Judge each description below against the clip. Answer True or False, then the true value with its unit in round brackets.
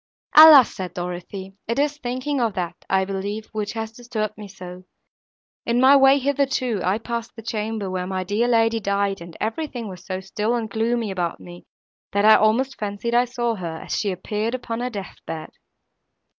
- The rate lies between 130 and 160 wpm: False (190 wpm)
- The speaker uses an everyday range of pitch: True (3.9 semitones)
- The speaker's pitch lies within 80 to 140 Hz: False (215 Hz)